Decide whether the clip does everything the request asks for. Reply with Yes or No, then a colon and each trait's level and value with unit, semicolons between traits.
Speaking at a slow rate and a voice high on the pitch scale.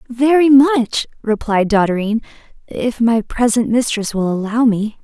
Yes: slow, 130 wpm; high, 230 Hz